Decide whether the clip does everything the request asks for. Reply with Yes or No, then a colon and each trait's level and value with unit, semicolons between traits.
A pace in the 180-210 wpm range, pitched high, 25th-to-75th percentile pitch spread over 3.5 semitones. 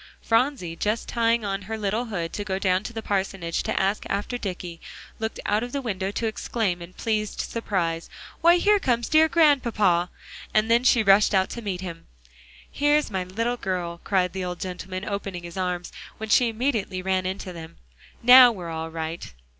Yes: average, 185 wpm; high, 200 Hz; average, 4.1 semitones